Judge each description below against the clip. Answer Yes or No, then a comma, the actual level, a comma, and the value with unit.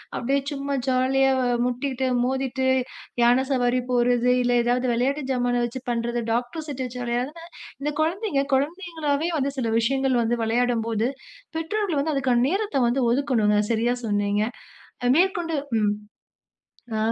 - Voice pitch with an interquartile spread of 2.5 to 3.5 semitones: Yes, average, 2.9 semitones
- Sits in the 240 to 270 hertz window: Yes, very high, 260 Hz